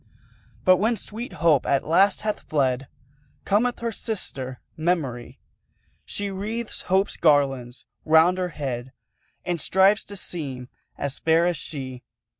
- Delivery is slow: Yes, slow, 130 wpm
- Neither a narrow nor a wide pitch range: No, wide, 6.6 semitones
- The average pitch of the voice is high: No, medium, 165 Hz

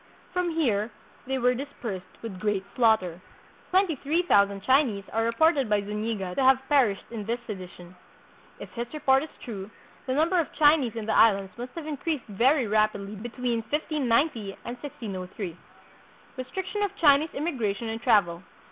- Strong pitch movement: Yes, wide, 5.9 semitones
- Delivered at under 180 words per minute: Yes, average, 160 wpm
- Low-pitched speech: No, high, 235 Hz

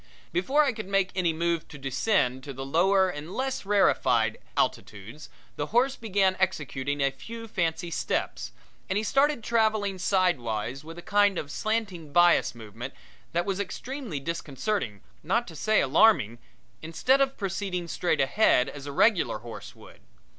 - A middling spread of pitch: No, wide, 6.9 semitones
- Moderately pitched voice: Yes, medium, 175 Hz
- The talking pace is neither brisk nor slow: Yes, average, 160 wpm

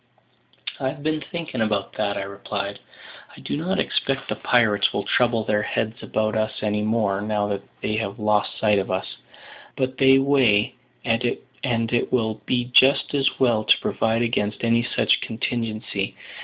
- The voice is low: Yes, low, 115 Hz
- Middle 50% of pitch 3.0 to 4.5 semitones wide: Yes, average, 3.3 semitones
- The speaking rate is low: No, average, 165 wpm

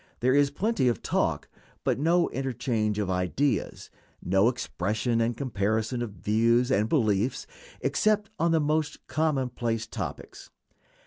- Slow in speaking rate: Yes, slow, 130 wpm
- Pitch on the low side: Yes, low, 120 Hz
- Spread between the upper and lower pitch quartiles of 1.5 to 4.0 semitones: No, average, 4.8 semitones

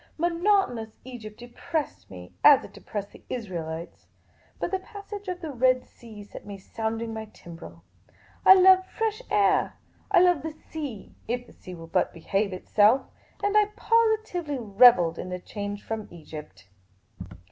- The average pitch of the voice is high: Yes, high, 235 Hz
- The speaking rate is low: No, average, 155 wpm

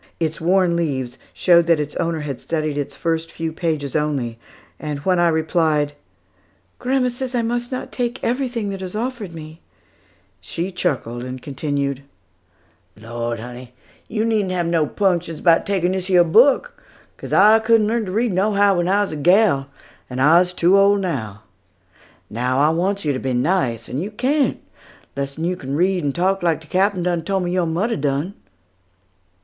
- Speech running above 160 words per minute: Yes, average, 180 wpm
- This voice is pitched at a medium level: Yes, medium, 170 Hz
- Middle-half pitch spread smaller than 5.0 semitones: No, average, 5.3 semitones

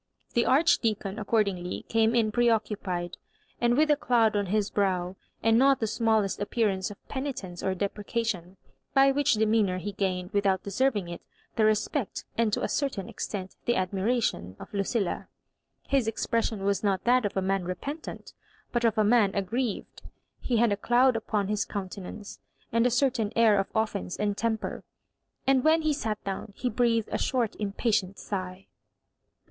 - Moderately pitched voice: No, high, 215 Hz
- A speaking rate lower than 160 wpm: No, average, 170 wpm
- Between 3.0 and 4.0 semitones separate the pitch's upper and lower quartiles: Yes, average, 3.4 semitones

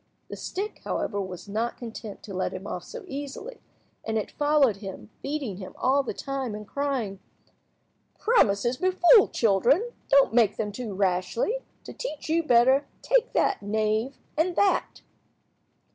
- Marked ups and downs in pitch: Yes, wide, 6.7 semitones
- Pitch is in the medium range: No, high, 245 Hz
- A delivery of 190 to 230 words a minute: No, average, 150 wpm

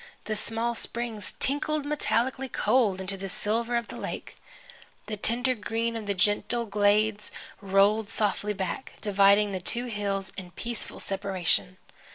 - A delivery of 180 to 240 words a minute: No, average, 145 wpm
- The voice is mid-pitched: No, high, 210 Hz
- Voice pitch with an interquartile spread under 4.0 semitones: Yes, average, 2.9 semitones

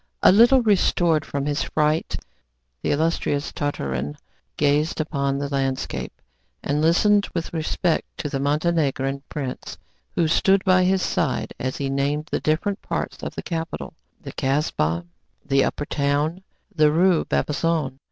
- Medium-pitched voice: Yes, medium, 150 Hz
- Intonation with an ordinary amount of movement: Yes, average, 3.3 semitones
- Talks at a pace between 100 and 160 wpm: Yes, average, 150 wpm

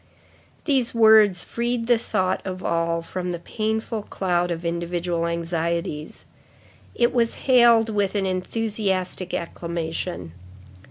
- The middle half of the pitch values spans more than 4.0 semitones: Yes, average, 4.7 semitones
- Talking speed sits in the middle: No, slow, 115 wpm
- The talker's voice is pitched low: No, medium, 185 Hz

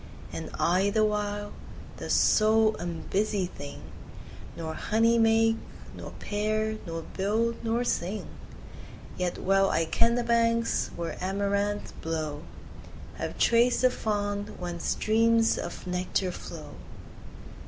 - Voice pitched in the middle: No, high, 205 Hz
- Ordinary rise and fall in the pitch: Yes, average, 3.7 semitones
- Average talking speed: No, slow, 120 wpm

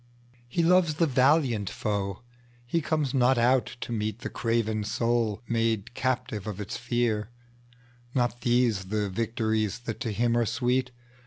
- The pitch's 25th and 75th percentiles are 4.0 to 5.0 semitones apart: No, narrow, 2.5 semitones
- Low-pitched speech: Yes, low, 120 Hz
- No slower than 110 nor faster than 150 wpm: Yes, average, 140 wpm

